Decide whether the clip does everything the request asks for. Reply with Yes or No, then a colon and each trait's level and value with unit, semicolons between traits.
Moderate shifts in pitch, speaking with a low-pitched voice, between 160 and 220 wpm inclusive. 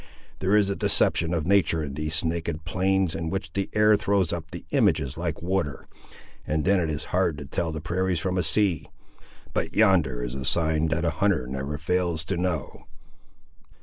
Yes: average, 3.4 semitones; very low, 85 Hz; average, 190 wpm